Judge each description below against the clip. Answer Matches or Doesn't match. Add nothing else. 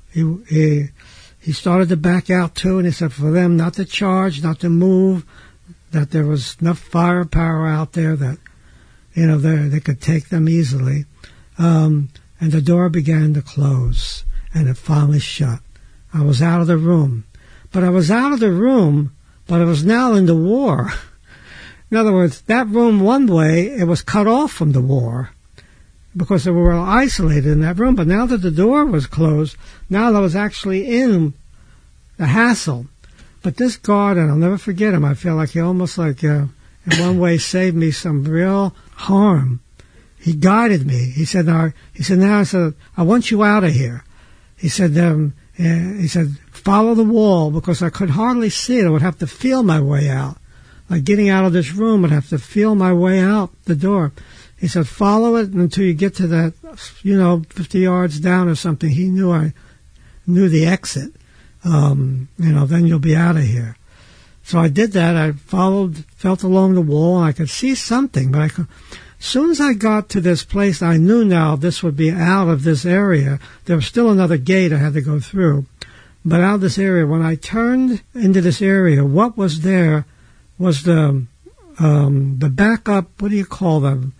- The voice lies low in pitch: Doesn't match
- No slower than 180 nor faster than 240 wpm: Matches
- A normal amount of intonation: Matches